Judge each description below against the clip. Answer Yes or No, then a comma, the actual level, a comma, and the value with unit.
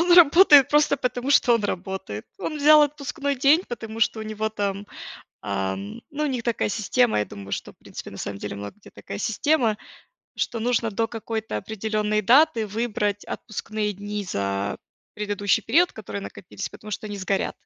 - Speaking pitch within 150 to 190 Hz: No, high, 220 Hz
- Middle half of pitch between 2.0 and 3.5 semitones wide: No, average, 4.4 semitones